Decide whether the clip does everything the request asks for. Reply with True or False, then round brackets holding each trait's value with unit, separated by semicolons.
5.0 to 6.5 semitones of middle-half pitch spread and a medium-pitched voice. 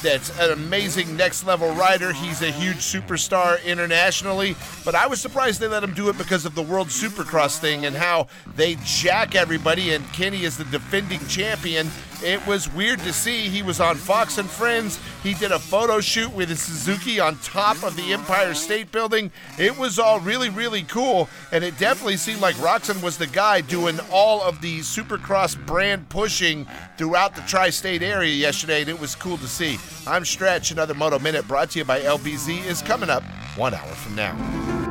False (3.7 semitones; 180 Hz)